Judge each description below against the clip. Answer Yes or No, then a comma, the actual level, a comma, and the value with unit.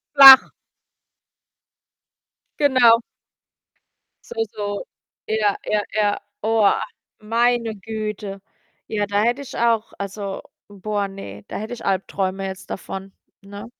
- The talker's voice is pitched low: No, high, 210 Hz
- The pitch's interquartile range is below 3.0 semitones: Yes, narrow, 2.5 semitones